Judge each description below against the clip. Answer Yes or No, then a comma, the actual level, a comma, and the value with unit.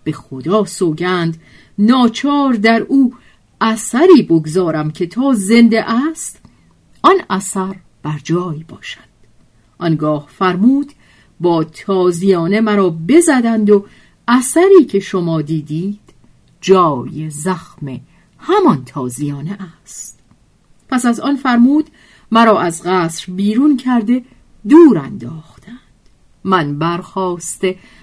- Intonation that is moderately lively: No, wide, 6.7 semitones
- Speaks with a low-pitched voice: No, high, 190 Hz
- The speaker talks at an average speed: No, slow, 100 wpm